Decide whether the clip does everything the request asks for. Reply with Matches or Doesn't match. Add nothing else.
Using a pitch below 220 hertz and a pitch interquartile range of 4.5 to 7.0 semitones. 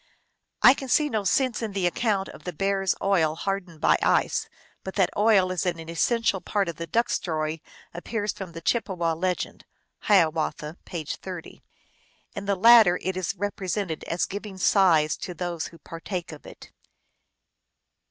Doesn't match